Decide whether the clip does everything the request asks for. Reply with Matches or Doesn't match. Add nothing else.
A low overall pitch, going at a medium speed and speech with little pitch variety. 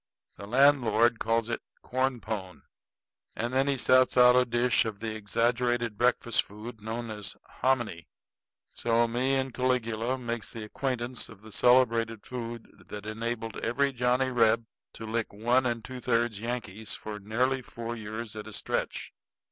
Matches